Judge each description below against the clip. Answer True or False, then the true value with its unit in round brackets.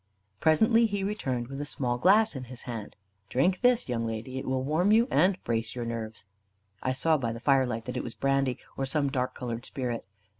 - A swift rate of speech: True (210 wpm)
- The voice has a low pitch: True (130 Hz)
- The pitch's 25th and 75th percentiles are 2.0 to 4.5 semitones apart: False (5.0 semitones)